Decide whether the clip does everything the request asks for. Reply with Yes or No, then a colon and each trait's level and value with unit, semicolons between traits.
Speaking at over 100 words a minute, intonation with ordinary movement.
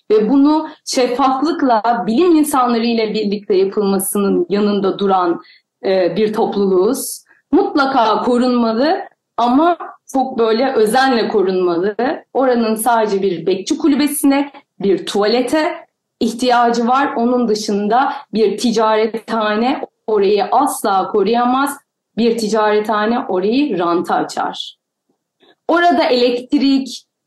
No: slow, 95 wpm; average, 4.5 semitones